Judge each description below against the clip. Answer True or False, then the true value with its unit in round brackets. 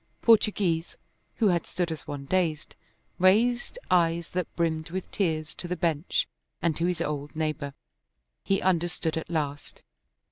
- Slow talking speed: False (145 wpm)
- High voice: False (170 Hz)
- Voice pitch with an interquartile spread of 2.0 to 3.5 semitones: True (2.7 semitones)